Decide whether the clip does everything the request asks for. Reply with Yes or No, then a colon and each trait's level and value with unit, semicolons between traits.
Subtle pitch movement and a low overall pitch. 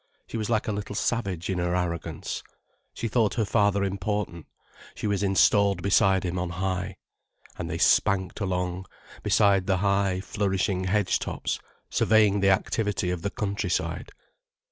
Yes: narrow, 2.0 semitones; low, 100 Hz